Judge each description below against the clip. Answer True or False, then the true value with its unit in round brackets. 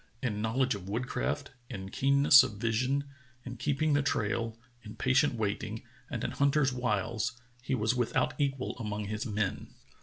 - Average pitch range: True (3.9 semitones)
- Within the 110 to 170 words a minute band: True (160 wpm)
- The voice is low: True (120 Hz)